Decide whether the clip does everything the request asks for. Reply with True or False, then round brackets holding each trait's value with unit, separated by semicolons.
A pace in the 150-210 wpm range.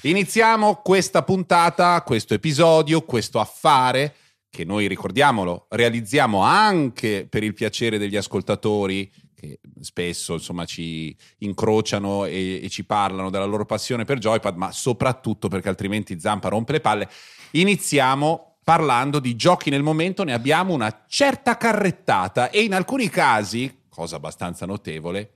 False (135 wpm)